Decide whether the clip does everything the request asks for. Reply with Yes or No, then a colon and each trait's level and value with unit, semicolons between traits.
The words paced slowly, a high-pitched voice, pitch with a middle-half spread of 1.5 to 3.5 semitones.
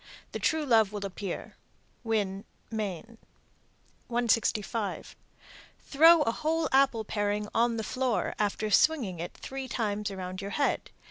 No: slow, 130 wpm; high, 220 Hz; average, 4.3 semitones